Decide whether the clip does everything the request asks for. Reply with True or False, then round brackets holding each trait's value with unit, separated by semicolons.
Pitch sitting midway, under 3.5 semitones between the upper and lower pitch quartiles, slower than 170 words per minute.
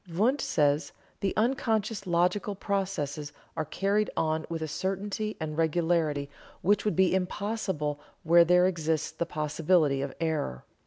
False (170 Hz; 4.3 semitones; 140 wpm)